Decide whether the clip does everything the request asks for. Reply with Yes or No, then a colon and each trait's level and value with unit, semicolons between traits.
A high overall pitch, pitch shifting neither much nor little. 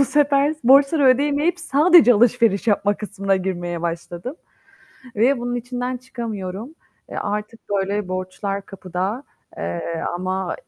No: high, 215 Hz; wide, 5.8 semitones